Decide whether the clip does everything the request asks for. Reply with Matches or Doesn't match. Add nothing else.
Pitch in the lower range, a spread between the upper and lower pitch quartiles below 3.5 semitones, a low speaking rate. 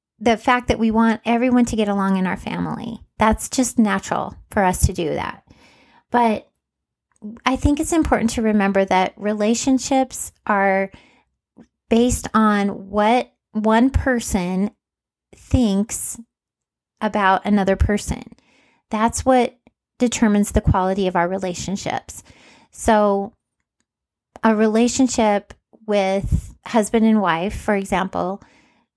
Doesn't match